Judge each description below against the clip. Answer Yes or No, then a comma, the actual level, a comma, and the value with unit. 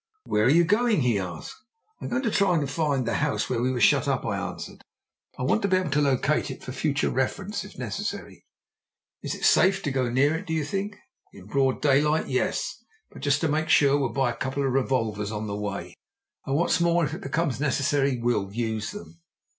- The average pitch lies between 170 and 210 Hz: No, medium, 140 Hz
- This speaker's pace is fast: Yes, fast, 220 wpm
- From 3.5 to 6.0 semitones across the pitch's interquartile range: Yes, average, 4.8 semitones